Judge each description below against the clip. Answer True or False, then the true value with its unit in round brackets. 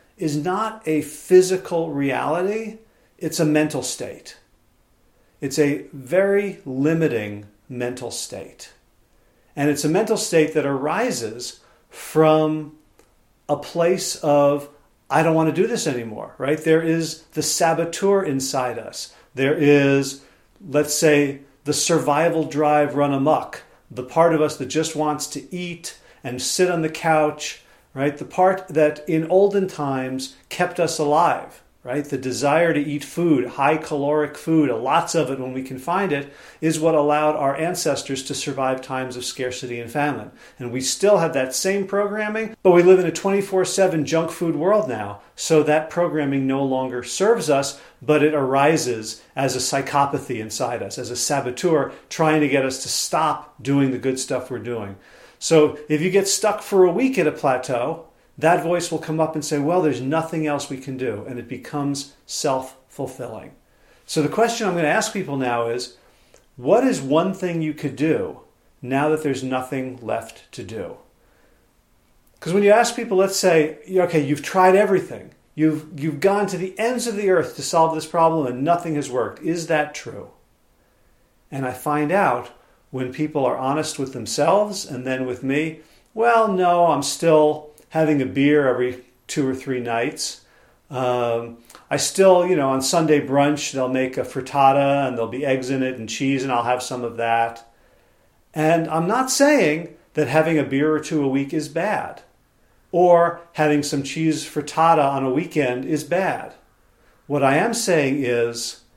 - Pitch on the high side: False (150 Hz)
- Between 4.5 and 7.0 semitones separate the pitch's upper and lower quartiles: False (3.8 semitones)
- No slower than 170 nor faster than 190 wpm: True (175 wpm)